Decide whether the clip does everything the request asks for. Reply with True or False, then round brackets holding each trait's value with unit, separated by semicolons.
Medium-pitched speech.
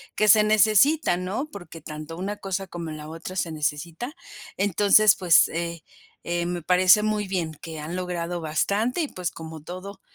True (180 Hz)